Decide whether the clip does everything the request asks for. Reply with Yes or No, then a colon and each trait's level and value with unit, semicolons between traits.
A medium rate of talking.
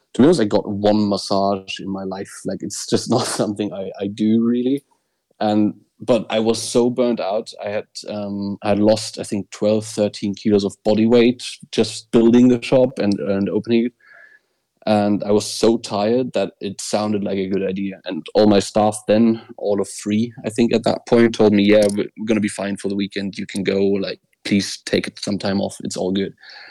No: fast, 215 wpm